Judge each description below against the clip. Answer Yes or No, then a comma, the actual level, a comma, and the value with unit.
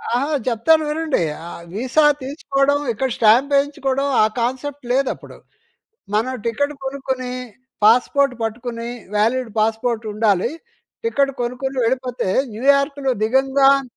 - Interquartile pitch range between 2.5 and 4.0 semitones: Yes, average, 3.1 semitones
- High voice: Yes, very high, 260 Hz